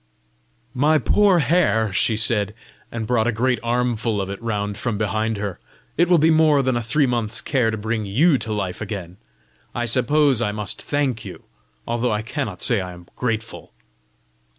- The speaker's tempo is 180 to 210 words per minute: Yes, average, 185 wpm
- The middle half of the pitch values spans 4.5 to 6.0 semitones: No, average, 3.7 semitones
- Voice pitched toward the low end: Yes, low, 115 Hz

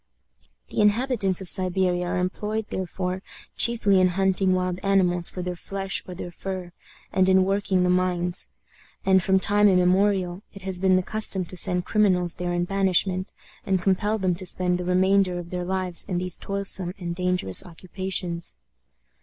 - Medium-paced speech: Yes, average, 170 wpm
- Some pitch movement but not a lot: No, narrow, 1.4 semitones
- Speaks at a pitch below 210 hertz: Yes, medium, 185 Hz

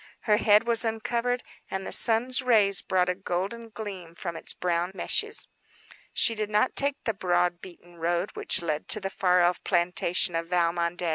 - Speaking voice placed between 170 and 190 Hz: Yes, medium, 185 Hz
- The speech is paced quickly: No, average, 180 wpm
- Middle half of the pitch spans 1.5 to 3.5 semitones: No, average, 4.0 semitones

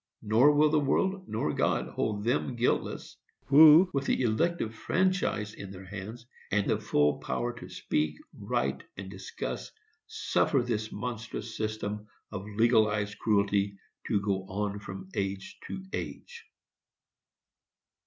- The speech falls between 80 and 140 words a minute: Yes, slow, 135 wpm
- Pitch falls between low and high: No, low, 110 Hz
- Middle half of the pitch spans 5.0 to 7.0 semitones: No, average, 3.9 semitones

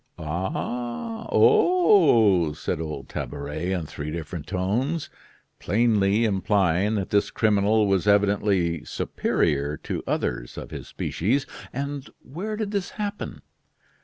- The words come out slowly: Yes, slow, 115 wpm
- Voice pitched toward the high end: No, low, 100 Hz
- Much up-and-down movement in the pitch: Yes, wide, 8.0 semitones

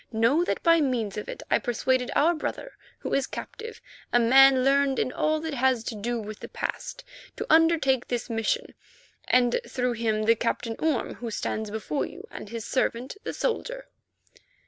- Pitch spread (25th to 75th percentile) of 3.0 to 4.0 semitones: No, average, 4.9 semitones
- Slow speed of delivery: No, average, 180 wpm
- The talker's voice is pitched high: Yes, very high, 255 Hz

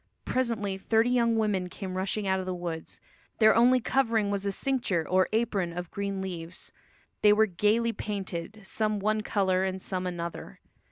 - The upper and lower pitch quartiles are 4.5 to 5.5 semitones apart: No, average, 2.9 semitones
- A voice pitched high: Yes, high, 200 Hz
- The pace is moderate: Yes, average, 170 wpm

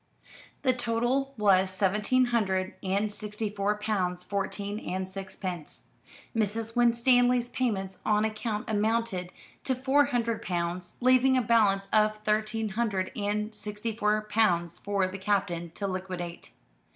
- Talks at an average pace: No, slow, 130 wpm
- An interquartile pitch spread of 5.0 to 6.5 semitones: No, average, 3.3 semitones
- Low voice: No, high, 210 Hz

